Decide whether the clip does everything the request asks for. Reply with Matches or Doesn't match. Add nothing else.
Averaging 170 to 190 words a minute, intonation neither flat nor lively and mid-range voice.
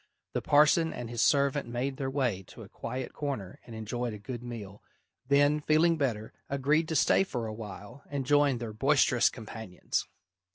Doesn't match